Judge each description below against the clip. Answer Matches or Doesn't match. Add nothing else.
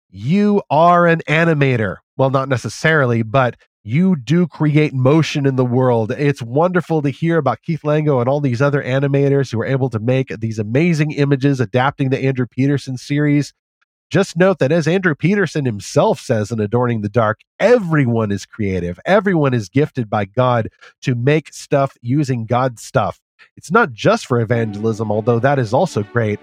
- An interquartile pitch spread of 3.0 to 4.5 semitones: Matches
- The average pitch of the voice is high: Doesn't match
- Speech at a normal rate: Matches